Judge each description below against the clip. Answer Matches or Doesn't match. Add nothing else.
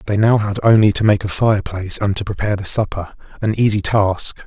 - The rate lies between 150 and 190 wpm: Doesn't match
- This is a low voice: Matches